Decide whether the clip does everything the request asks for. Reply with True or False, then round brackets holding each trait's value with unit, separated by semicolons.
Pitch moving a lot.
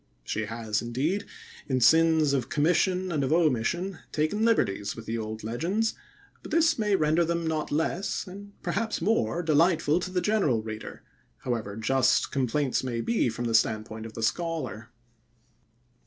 True (7.6 semitones)